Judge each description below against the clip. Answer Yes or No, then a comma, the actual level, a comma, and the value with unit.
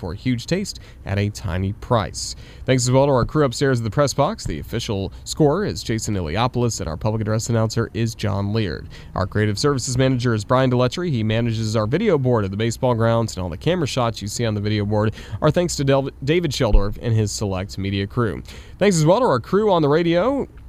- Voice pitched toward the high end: No, low, 115 Hz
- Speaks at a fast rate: Yes, fast, 230 wpm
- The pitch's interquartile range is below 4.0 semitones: No, average, 4.6 semitones